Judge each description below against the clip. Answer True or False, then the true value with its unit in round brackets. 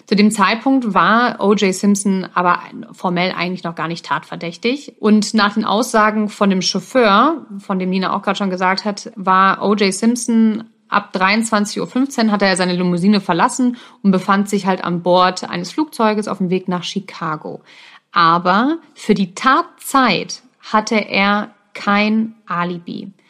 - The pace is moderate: True (155 wpm)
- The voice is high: True (205 Hz)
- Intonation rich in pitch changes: False (3.4 semitones)